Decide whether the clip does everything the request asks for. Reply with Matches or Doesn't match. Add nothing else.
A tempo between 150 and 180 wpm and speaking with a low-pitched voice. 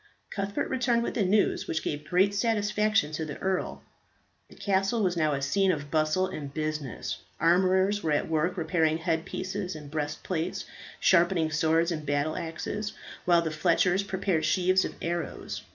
Doesn't match